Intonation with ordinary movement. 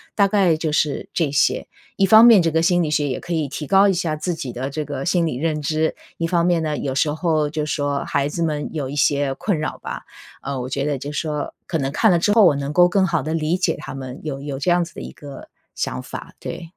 Yes: average, 3.3 semitones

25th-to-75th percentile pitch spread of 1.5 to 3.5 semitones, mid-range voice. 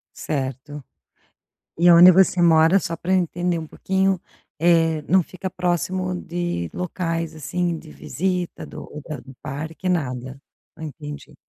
Yes: average, 2.9 semitones; medium, 170 Hz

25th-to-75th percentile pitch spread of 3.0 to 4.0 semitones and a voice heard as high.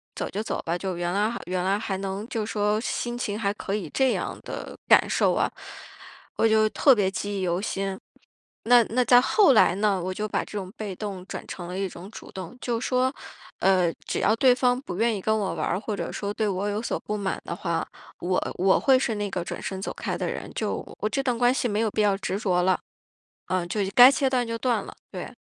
Yes: average, 3.3 semitones; high, 205 Hz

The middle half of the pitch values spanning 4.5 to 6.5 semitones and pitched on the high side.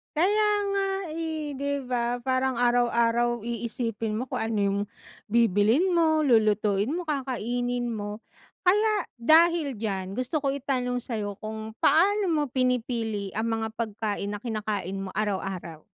Yes: average, 4.8 semitones; high, 240 Hz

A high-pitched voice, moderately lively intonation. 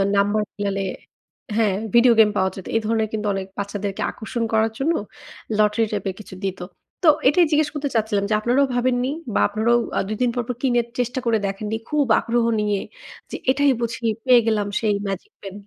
Yes: high, 220 Hz; average, 3.2 semitones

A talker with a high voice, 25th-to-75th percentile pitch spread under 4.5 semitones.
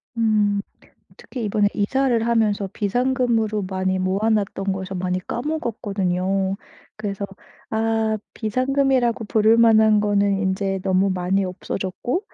Yes: high, 210 Hz; average, 2.9 semitones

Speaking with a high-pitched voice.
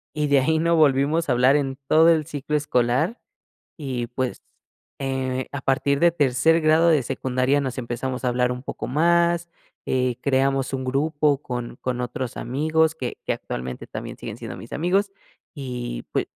No: low, 135 Hz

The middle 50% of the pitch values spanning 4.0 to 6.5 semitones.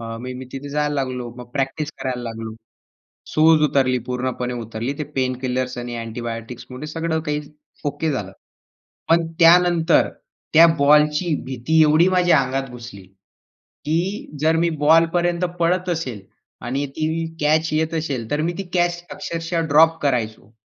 Yes: average, 4.5 semitones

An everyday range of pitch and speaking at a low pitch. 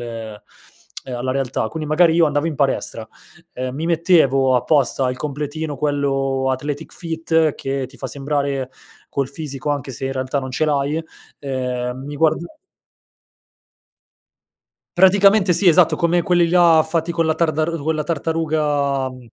No: average, 3.4 semitones; medium, 145 Hz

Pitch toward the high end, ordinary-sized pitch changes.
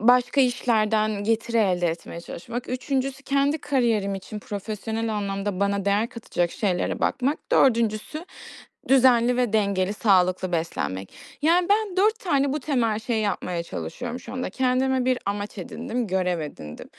Yes: high, 225 Hz; average, 4.4 semitones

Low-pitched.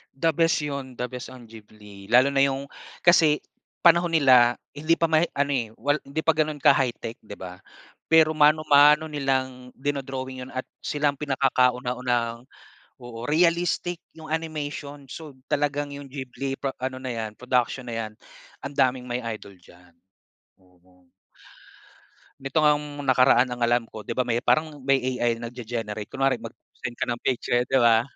Yes: low, 130 Hz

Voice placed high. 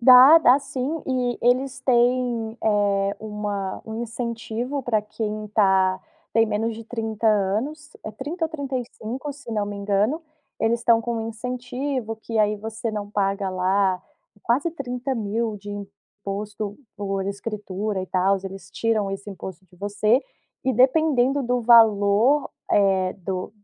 Yes: high, 220 Hz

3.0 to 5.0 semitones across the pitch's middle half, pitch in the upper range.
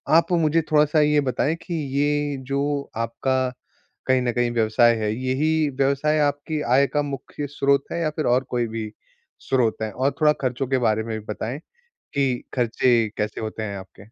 No: average, 3.9 semitones; low, 130 Hz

